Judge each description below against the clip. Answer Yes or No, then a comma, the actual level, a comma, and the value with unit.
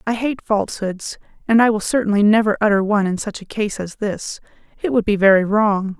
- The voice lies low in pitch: No, high, 210 Hz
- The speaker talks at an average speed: No, fast, 210 wpm